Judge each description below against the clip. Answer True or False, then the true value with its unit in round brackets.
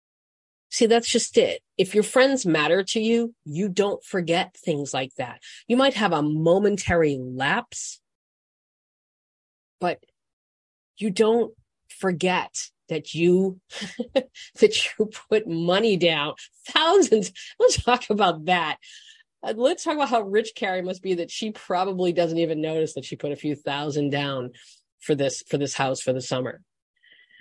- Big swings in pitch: True (6.8 semitones)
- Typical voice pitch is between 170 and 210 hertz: True (190 Hz)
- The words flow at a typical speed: True (145 wpm)